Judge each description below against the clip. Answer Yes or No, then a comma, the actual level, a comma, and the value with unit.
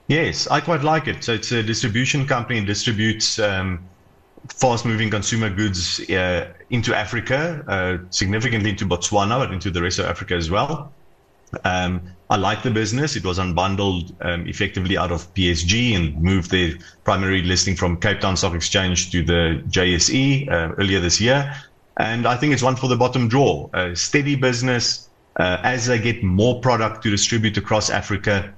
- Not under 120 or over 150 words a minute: No, average, 175 wpm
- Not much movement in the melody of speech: No, average, 4.8 semitones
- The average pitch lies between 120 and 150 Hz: No, low, 105 Hz